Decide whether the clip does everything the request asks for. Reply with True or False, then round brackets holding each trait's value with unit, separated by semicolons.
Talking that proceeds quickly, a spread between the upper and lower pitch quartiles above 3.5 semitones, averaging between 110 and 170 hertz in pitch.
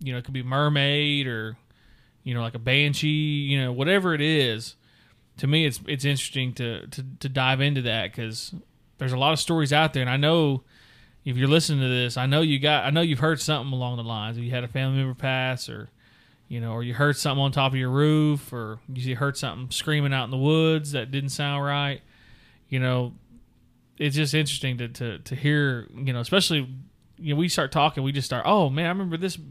False (230 wpm; 2.9 semitones; 135 Hz)